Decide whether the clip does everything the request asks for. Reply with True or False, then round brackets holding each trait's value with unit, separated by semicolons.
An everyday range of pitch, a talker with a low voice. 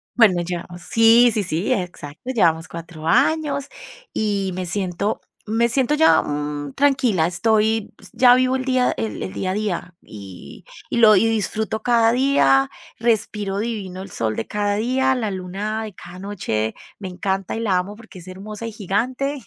False (4.6 semitones; 205 Hz)